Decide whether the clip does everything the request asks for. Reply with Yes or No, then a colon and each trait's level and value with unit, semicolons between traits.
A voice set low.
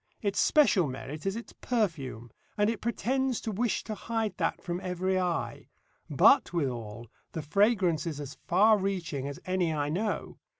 No: medium, 185 Hz